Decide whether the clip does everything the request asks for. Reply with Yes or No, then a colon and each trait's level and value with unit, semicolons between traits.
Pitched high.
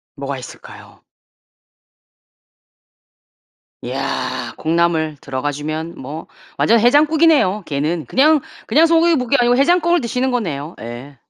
Yes: high, 210 Hz